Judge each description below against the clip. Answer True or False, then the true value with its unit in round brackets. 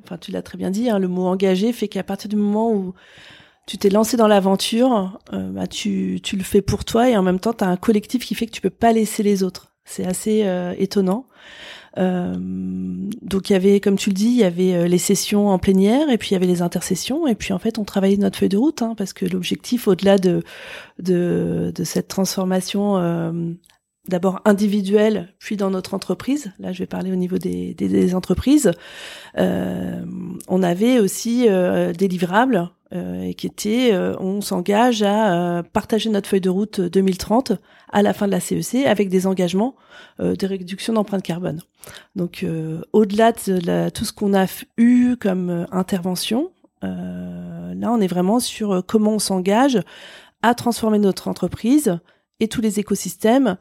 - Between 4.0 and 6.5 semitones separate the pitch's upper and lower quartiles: False (3.1 semitones)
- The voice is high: True (195 Hz)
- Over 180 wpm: True (195 wpm)